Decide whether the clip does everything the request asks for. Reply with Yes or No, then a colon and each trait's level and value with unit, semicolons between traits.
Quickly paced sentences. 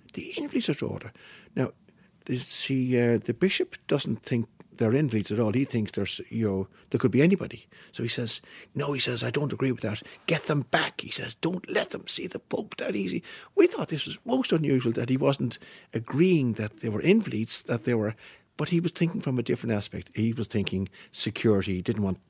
Yes: fast, 210 wpm